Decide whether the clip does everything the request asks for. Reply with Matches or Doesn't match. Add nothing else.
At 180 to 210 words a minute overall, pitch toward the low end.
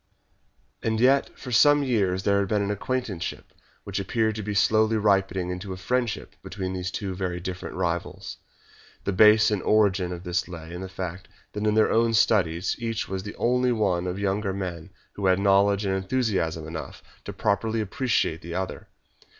Matches